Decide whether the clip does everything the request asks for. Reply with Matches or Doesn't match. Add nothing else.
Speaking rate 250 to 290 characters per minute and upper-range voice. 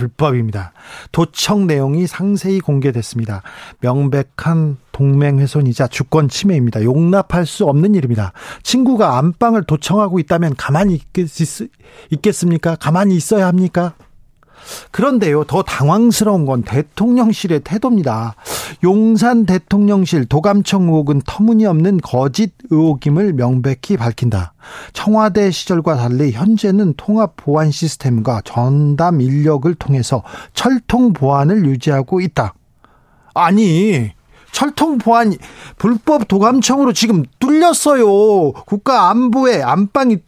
Doesn't match